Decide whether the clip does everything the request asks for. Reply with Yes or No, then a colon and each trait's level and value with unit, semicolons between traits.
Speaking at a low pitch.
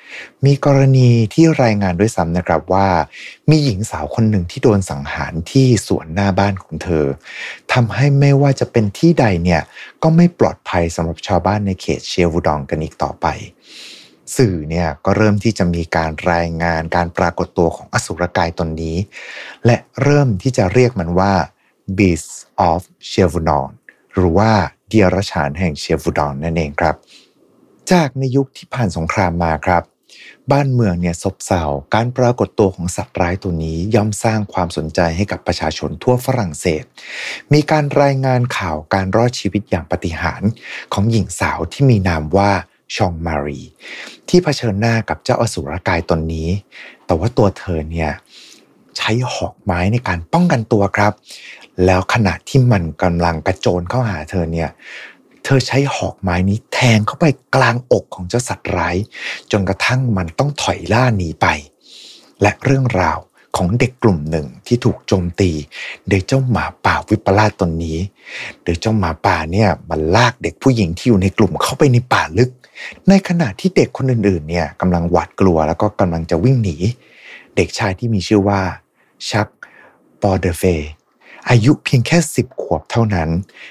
Yes: very low, 95 Hz